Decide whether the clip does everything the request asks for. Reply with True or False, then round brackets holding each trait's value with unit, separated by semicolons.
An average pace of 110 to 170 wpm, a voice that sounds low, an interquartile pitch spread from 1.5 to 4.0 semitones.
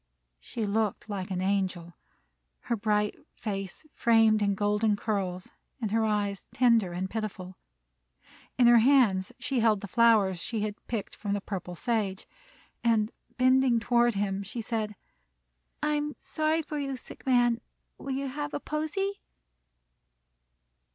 False (145 wpm; 220 Hz; 3.5 semitones)